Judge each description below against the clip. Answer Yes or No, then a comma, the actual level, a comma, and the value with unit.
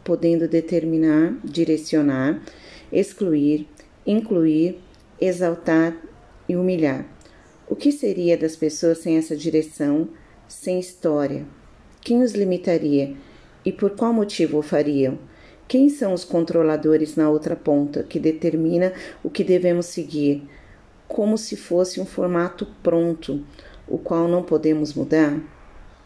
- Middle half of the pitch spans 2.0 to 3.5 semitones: Yes, average, 2.8 semitones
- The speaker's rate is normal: No, slow, 115 wpm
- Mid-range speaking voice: Yes, medium, 165 Hz